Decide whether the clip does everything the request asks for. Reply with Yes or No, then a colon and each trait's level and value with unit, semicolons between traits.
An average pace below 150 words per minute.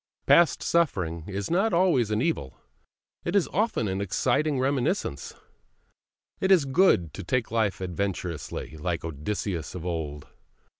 Yes: slow, 135 wpm